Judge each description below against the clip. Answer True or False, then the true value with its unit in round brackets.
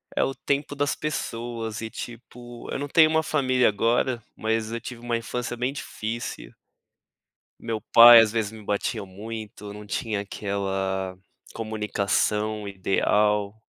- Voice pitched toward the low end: True (110 Hz)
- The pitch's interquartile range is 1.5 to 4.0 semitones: True (2.6 semitones)